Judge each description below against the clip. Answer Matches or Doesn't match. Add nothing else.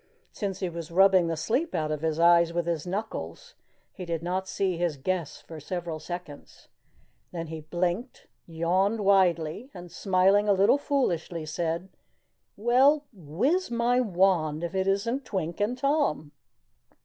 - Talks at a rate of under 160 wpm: Matches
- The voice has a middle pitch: Matches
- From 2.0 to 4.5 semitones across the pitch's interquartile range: Matches